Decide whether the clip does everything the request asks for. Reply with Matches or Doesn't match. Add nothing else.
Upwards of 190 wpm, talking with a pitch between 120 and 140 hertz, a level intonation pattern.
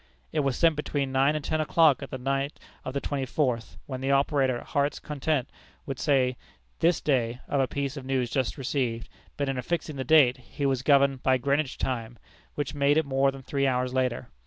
Matches